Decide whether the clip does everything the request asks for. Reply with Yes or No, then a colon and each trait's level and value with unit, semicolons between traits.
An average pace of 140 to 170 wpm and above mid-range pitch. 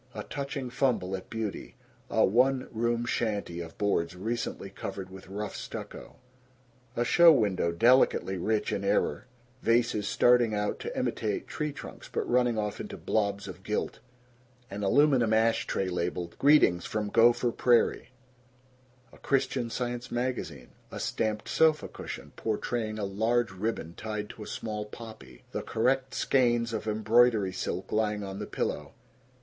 No: average, 150 wpm; low, 110 Hz